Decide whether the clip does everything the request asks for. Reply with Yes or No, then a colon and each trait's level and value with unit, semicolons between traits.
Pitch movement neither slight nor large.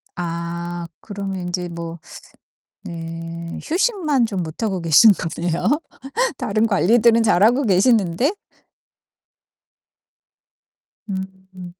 Yes: average, 4.8 semitones